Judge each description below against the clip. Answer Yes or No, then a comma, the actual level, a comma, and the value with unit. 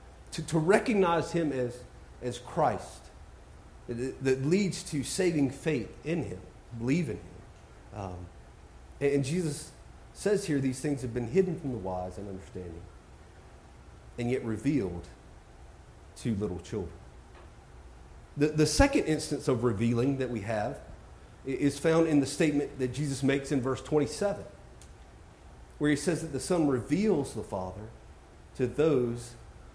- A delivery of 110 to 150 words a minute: Yes, average, 140 wpm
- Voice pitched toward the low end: Yes, low, 130 Hz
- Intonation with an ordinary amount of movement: No, wide, 8.3 semitones